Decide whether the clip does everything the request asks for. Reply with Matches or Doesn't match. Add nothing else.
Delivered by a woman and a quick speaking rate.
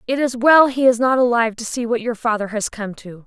Matches